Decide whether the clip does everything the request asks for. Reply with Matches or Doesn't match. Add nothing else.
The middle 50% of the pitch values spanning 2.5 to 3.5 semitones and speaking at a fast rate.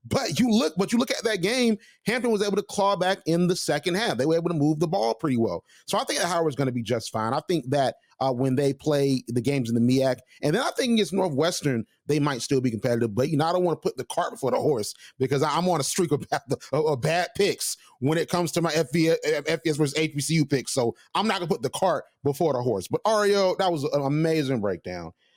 Doesn't match